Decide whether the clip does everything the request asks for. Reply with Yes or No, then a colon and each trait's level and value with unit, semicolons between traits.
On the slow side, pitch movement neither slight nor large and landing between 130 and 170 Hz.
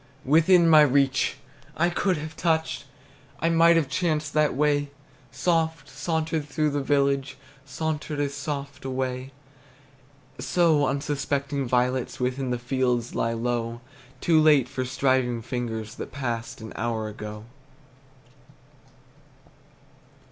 Yes: slow, 120 wpm; average, 3.6 semitones; medium, 140 Hz